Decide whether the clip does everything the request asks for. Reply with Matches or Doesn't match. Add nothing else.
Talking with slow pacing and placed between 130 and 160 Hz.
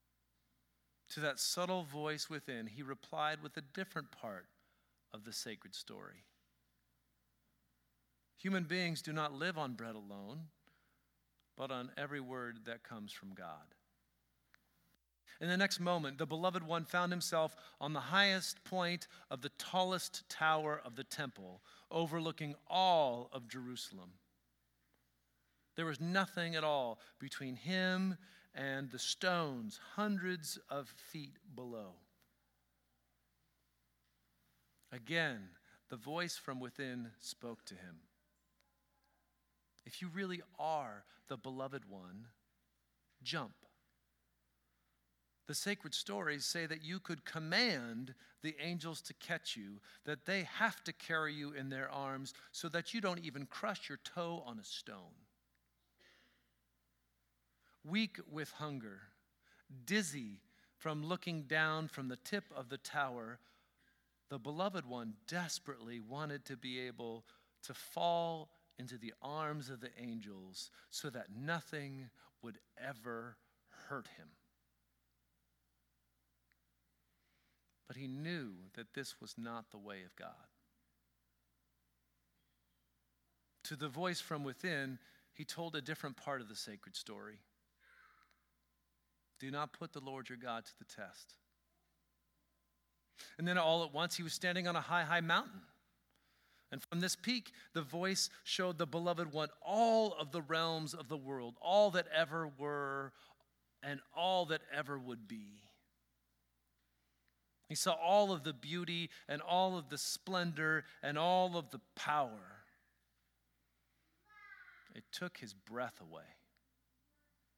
Matches